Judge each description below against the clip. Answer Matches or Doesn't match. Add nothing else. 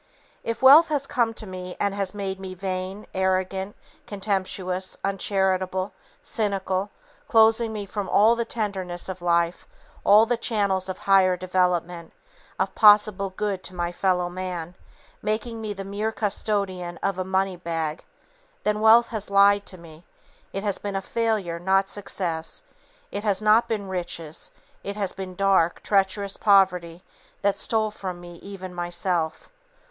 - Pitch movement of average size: Doesn't match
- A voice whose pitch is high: Matches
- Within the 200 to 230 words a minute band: Doesn't match